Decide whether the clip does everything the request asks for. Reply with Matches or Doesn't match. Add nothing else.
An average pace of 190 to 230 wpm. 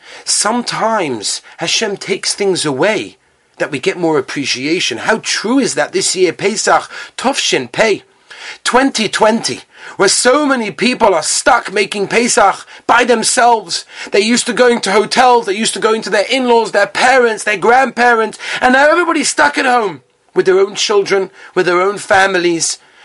Doesn't match